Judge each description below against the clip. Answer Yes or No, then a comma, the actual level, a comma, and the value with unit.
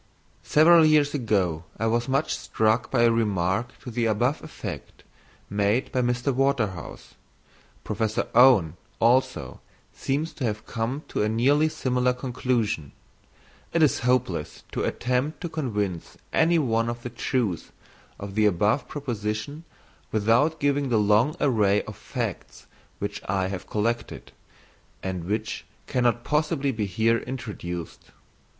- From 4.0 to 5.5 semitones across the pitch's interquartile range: Yes, average, 4.3 semitones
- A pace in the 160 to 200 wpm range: No, slow, 135 wpm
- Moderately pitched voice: No, low, 120 Hz